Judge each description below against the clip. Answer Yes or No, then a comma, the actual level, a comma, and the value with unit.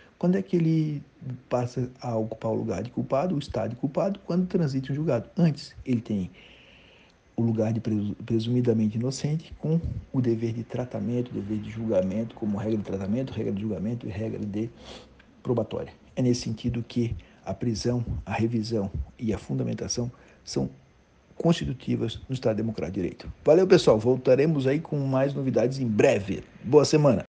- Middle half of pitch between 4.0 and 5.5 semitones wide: No, average, 3.6 semitones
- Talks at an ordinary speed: Yes, average, 165 wpm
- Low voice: Yes, low, 120 Hz